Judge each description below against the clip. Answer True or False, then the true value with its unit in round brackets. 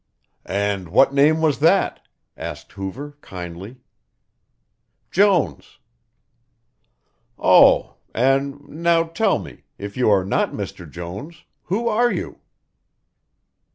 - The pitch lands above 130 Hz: True (140 Hz)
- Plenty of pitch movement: True (8.9 semitones)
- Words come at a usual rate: False (100 wpm)